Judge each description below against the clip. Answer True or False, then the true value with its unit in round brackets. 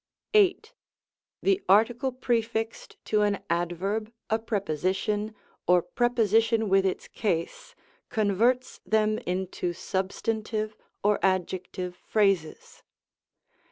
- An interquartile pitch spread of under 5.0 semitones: True (3.3 semitones)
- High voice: True (210 Hz)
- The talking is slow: True (95 wpm)